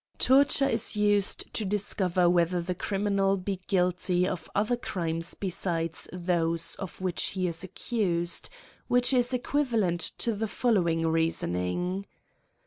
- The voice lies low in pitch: No, medium, 185 Hz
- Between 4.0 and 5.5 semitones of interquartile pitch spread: No, average, 3.3 semitones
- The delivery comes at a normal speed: No, slow, 130 wpm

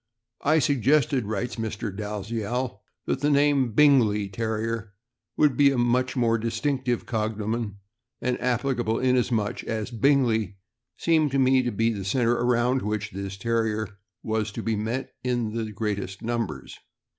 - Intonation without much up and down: No, average, 3.0 semitones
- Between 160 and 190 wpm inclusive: No, average, 145 wpm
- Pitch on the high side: No, low, 115 Hz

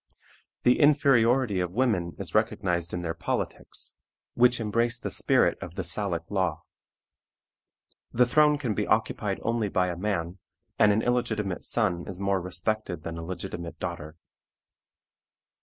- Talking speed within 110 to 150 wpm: Yes, average, 140 wpm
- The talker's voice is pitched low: Yes, low, 100 Hz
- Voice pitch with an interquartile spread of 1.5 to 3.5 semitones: No, average, 5.2 semitones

